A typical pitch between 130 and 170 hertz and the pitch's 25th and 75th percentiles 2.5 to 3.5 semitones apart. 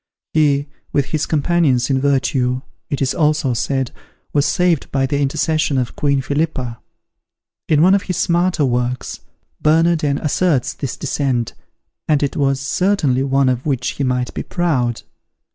Yes: medium, 140 Hz; average, 3.2 semitones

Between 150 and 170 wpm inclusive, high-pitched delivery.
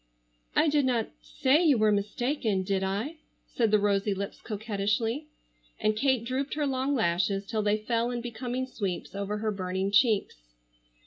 Yes: average, 165 wpm; high, 215 Hz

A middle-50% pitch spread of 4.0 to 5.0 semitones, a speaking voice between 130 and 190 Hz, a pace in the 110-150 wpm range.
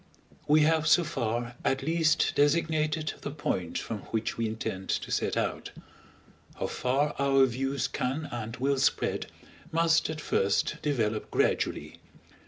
Yes: average, 4.6 semitones; medium, 140 Hz; average, 140 wpm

